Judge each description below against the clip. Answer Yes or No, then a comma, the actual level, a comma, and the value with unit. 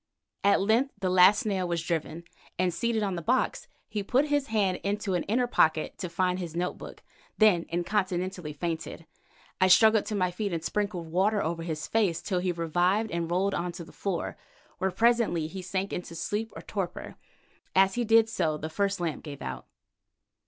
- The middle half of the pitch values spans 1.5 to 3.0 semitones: No, average, 3.6 semitones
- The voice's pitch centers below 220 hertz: Yes, medium, 185 Hz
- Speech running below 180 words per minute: No, average, 190 wpm